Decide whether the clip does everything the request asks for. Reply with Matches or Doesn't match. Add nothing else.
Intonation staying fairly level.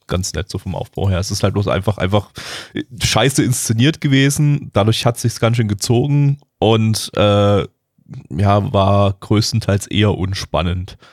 Doesn't match